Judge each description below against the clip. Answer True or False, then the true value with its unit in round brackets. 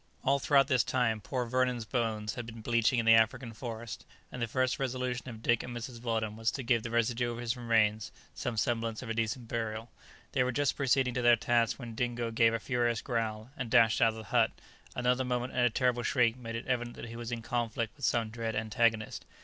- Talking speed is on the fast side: True (230 wpm)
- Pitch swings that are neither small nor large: False (1.7 semitones)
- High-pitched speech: False (120 Hz)